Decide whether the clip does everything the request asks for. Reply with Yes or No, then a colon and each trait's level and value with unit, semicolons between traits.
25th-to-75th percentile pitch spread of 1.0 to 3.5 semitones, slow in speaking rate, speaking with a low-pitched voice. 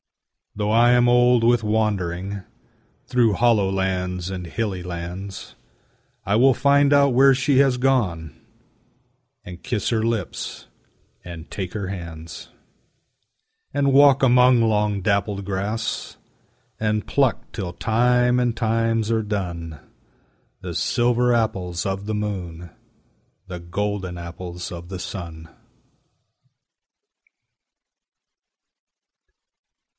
No: average, 5.0 semitones; slow, 110 wpm; low, 105 Hz